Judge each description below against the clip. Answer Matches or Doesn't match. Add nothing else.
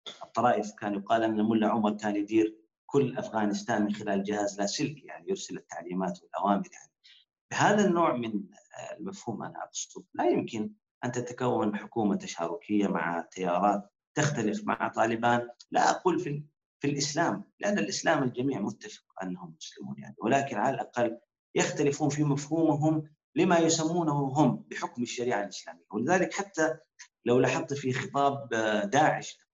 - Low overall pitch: Matches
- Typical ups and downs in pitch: Doesn't match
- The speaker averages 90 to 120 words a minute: Doesn't match